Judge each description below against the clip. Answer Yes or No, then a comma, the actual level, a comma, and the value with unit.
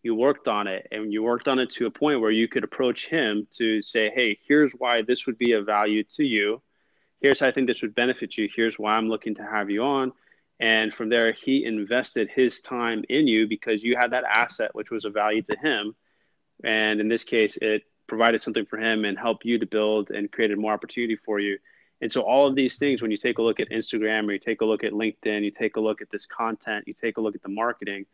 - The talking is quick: Yes, fast, 255 wpm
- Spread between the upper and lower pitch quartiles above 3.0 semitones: No, narrow, 2.5 semitones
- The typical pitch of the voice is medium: No, low, 110 Hz